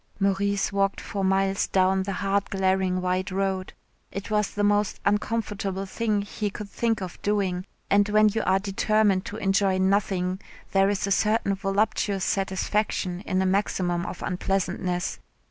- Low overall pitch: No, high, 195 Hz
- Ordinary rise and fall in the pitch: No, narrow, 1.4 semitones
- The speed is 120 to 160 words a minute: Yes, average, 155 wpm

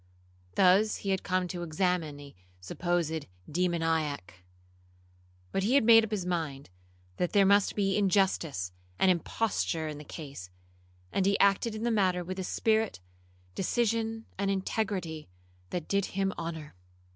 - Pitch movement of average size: Yes, average, 3.9 semitones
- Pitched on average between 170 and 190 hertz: Yes, medium, 185 Hz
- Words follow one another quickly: No, average, 145 wpm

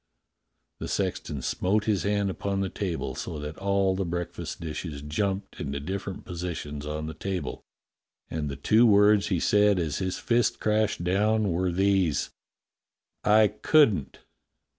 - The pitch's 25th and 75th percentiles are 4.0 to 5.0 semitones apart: Yes, average, 4.5 semitones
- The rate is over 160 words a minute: No, average, 150 wpm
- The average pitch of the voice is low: Yes, very low, 95 Hz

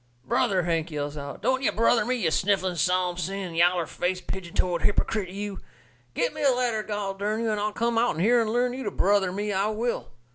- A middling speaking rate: No, fast, 220 wpm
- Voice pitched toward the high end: Yes, high, 200 Hz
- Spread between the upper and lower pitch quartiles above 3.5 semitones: Yes, average, 4.1 semitones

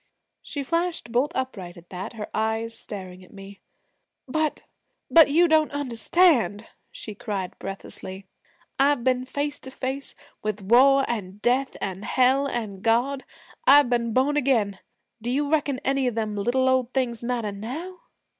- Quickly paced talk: No, average, 155 wpm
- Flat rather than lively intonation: No, average, 4.7 semitones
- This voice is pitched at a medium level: No, high, 245 Hz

